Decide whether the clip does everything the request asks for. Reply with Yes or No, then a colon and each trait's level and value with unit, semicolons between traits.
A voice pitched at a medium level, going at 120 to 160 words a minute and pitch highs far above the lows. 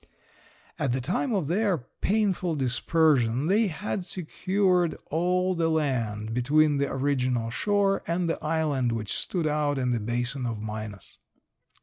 Yes: medium, 150 Hz; average, 140 wpm; wide, 6.5 semitones